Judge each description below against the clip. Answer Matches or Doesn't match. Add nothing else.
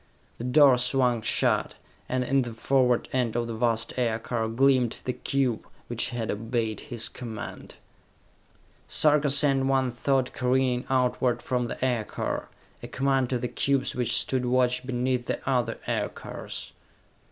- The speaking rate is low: Doesn't match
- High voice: Doesn't match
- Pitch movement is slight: Matches